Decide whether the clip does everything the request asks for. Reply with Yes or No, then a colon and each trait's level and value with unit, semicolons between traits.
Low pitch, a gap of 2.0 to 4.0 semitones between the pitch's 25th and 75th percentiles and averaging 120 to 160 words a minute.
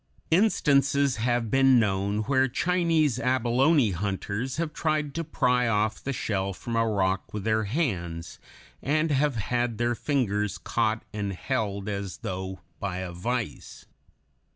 No: low, 115 Hz; wide, 5.5 semitones; average, 140 wpm